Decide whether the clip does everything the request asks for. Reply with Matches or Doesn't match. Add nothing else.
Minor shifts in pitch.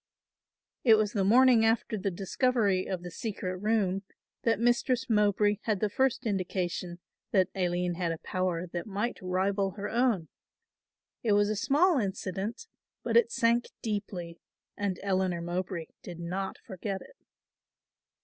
Doesn't match